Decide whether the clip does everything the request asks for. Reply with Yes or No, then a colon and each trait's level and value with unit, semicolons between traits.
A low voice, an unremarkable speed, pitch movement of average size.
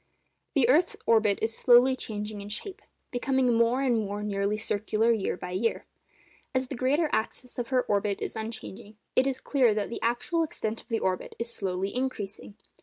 No: high, 230 Hz; average, 180 wpm; average, 3.6 semitones